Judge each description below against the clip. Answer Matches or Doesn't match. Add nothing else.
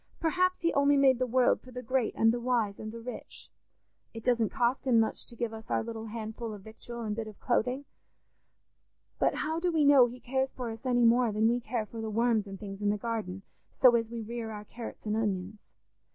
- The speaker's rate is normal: Doesn't match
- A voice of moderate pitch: Doesn't match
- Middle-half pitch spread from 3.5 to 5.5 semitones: Doesn't match